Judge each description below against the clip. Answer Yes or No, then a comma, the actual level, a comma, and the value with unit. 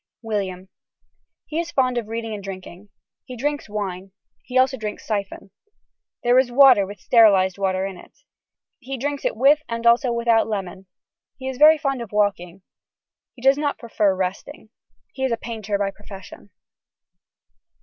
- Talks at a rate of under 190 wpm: Yes, average, 160 wpm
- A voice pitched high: Yes, high, 225 Hz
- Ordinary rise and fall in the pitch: Yes, average, 4.9 semitones